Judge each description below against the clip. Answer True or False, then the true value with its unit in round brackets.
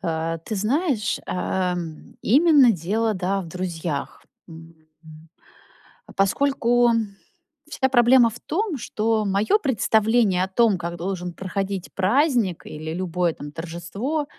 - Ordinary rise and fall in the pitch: False (5.8 semitones)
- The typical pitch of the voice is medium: False (195 Hz)